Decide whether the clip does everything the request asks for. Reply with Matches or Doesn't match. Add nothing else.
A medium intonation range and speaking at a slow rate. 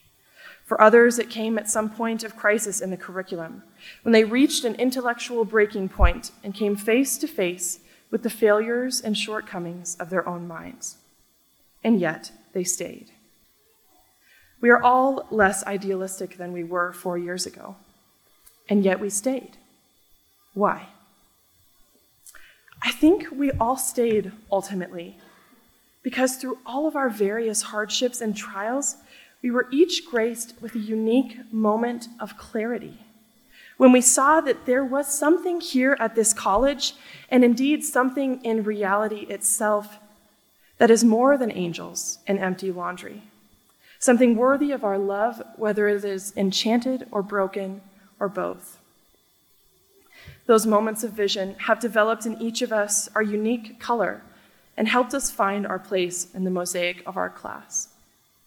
Doesn't match